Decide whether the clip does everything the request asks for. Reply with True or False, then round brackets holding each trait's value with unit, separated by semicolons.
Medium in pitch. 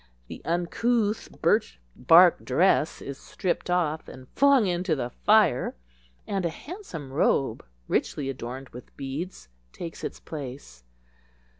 True (165 Hz)